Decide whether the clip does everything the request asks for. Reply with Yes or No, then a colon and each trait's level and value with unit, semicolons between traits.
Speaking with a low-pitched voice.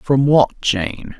Yes: low, 125 Hz